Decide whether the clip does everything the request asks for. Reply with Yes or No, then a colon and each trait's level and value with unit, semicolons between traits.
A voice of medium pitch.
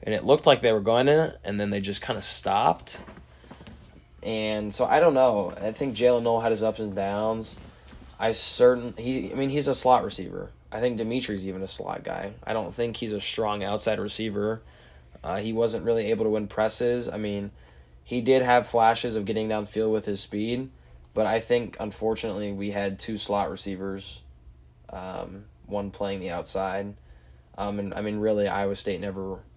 No: low, 105 Hz